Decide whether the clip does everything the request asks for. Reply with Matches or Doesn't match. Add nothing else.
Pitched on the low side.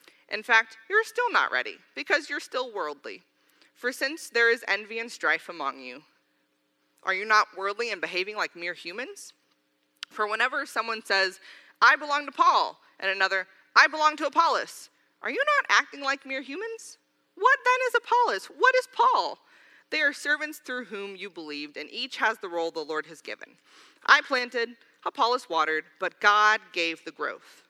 Doesn't match